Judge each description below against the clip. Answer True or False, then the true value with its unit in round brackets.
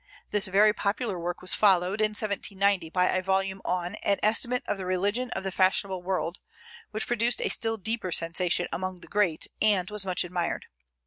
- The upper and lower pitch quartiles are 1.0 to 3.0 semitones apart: True (2.5 semitones)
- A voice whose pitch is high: True (195 Hz)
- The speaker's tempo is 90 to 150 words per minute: False (185 wpm)